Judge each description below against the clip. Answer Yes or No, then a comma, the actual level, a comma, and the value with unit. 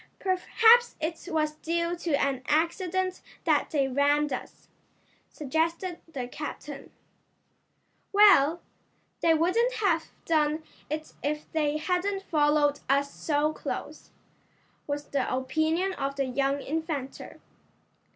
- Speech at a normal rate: No, slow, 110 wpm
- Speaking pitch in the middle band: No, very high, 310 Hz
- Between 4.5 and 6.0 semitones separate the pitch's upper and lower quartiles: No, average, 3.2 semitones